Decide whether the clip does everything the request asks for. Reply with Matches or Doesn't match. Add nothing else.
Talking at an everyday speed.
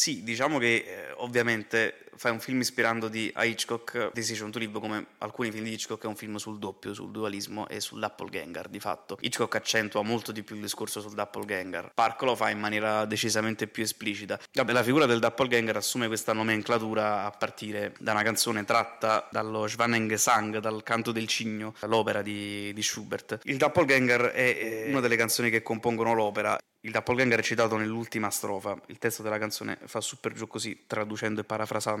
Doesn't match